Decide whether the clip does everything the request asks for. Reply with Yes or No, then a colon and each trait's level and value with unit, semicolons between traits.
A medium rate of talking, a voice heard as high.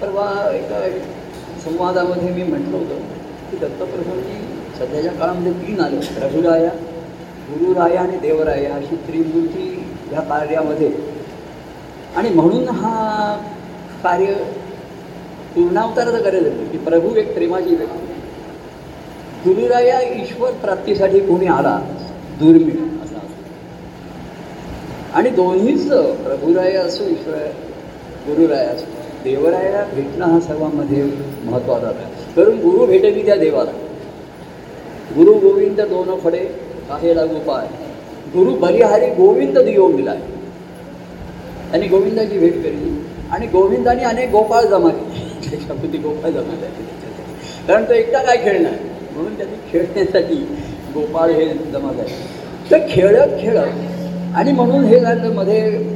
Yes: average, 110 wpm; high, 195 Hz